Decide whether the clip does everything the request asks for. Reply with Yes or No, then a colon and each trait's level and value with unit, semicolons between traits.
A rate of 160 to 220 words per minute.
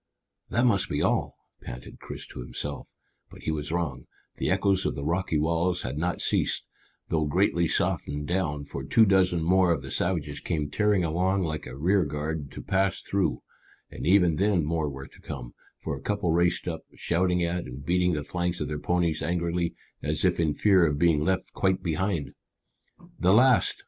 Yes: average, 185 wpm